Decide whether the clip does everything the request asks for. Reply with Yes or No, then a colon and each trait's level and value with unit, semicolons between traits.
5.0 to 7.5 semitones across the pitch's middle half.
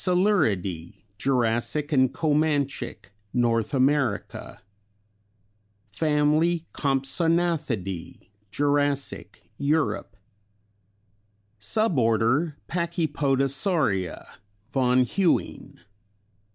Yes: wide, 5.5 semitones